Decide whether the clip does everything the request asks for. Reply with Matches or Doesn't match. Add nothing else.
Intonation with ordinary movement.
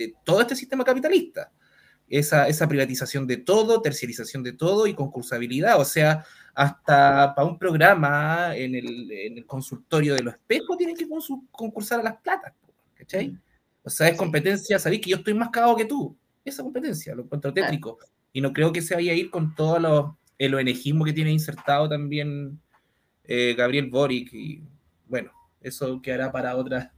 Doesn't match